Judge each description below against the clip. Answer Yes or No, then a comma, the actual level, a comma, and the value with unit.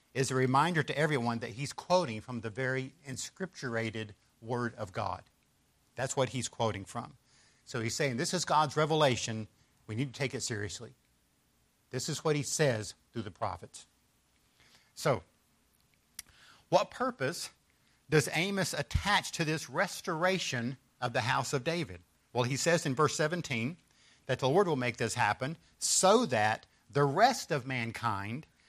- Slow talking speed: No, average, 155 wpm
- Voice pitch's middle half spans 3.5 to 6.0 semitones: Yes, average, 4.6 semitones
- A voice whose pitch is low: Yes, low, 130 Hz